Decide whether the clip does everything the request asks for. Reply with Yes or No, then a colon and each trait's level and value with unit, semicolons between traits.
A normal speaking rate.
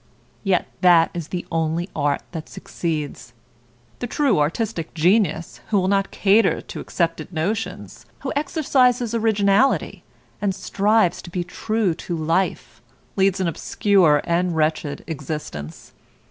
No: slow, 130 wpm